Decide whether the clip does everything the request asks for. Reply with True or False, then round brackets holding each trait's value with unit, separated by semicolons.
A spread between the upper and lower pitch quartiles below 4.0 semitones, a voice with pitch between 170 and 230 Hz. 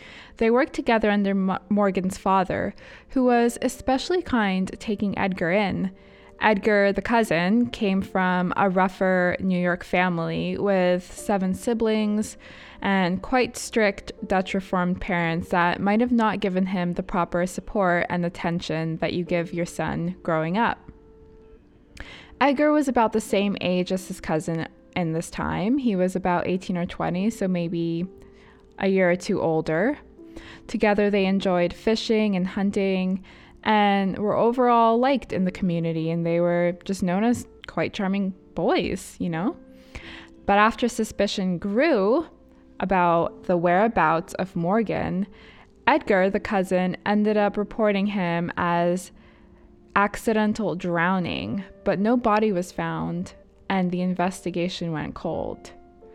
True (3.3 semitones; 190 Hz)